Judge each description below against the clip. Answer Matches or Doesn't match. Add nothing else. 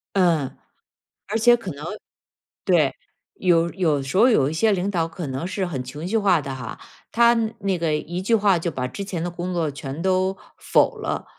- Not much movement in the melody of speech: Doesn't match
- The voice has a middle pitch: Matches